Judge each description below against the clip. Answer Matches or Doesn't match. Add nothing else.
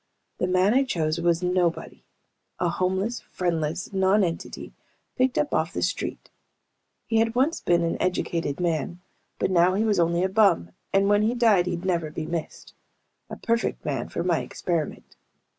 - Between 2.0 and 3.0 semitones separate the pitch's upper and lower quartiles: Doesn't match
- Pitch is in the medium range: Matches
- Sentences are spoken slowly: Doesn't match